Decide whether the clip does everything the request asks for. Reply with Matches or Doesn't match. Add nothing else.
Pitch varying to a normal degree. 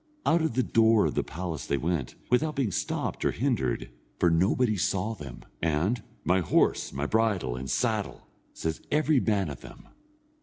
Doesn't match